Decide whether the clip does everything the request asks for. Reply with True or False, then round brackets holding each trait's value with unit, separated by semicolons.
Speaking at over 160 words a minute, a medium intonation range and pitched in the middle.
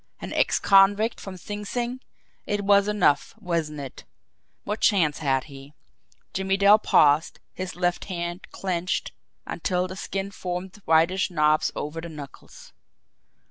False (140 wpm; 4.0 semitones; 180 Hz)